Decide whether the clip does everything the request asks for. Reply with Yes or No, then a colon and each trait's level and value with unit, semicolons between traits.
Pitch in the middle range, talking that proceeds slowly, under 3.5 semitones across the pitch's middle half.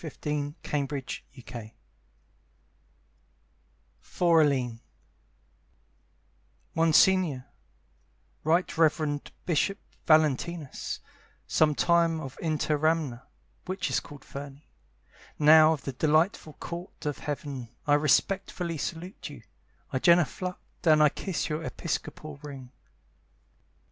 Yes: medium, 155 Hz; slow, 90 wpm; average, 2.7 semitones